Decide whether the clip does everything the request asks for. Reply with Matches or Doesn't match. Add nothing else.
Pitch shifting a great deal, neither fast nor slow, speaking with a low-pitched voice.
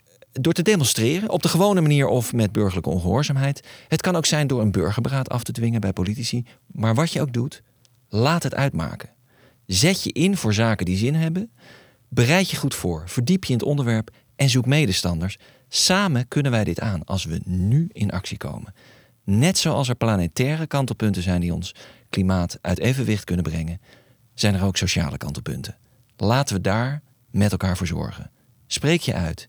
Matches